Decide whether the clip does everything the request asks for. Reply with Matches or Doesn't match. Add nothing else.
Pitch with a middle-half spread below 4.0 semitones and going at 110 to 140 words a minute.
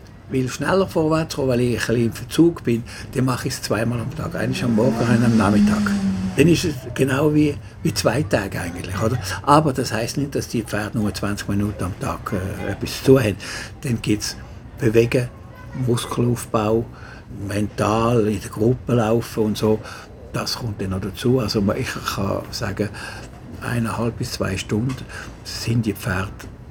Doesn't match